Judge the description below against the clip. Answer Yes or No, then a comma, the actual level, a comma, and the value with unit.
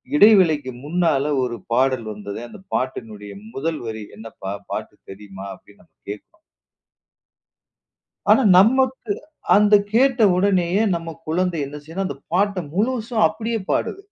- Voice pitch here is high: No, medium, 165 Hz